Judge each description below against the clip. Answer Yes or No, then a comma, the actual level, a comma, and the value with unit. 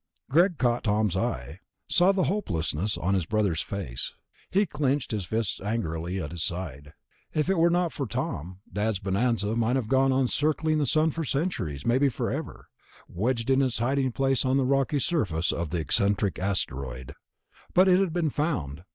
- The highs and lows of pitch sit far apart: Yes, wide, 7.5 semitones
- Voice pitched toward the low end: Yes, low, 115 Hz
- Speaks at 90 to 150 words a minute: No, average, 175 wpm